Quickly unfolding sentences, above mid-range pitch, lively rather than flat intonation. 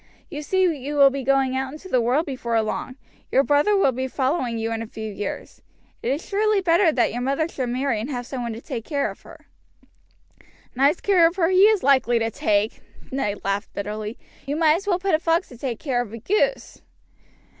Yes: fast, 225 wpm; very high, 270 Hz; wide, 5.8 semitones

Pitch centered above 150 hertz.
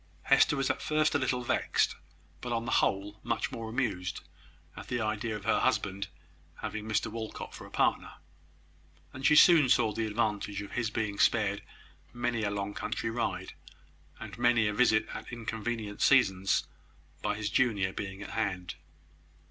No: low, 110 Hz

